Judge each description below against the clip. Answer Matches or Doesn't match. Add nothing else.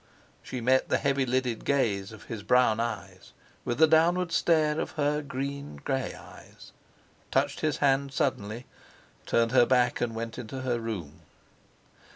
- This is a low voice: Matches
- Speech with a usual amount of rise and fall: Matches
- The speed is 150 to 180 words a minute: Matches